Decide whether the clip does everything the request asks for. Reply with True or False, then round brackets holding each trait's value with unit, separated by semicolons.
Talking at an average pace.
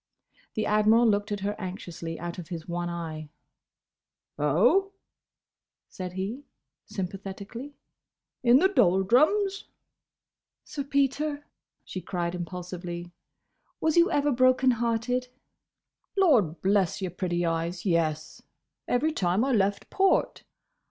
False (110 wpm)